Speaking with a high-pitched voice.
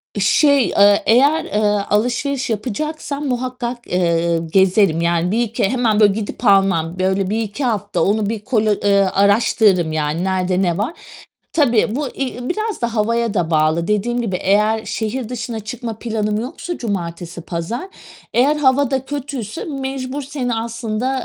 Yes: high, 220 Hz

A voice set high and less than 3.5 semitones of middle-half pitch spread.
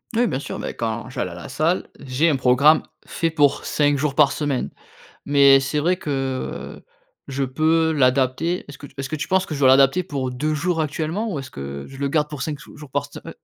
No: medium, 145 Hz; average, 2.7 semitones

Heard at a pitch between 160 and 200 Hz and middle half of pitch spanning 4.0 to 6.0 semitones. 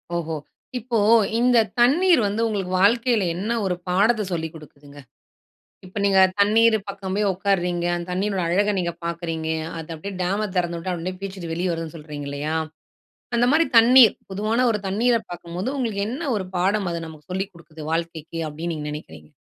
Yes: medium, 185 Hz; average, 4.3 semitones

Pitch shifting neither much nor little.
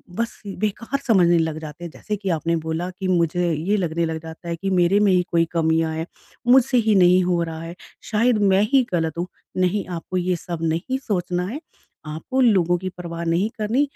Yes: average, 3.7 semitones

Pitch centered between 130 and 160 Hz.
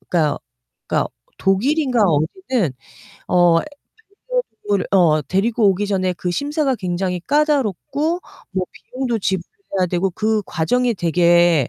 No: high, 195 Hz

